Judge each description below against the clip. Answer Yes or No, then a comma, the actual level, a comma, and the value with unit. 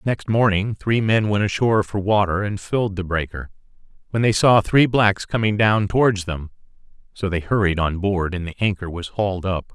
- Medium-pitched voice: No, low, 100 Hz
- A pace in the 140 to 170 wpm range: No, average, 195 wpm